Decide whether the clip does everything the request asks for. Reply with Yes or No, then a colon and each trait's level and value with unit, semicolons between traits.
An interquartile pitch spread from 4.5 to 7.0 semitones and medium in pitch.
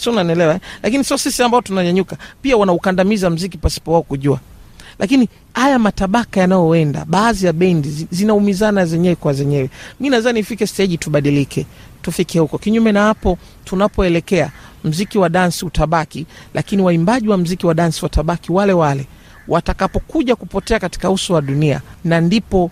No: average, 4.0 semitones; medium, 180 Hz